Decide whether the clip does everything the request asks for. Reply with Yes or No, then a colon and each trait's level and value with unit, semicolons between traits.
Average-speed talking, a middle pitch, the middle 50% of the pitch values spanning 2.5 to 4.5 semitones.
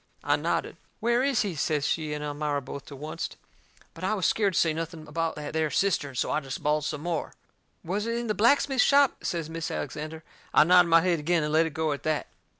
No: fast, 235 wpm; medium, 160 Hz; average, 3.6 semitones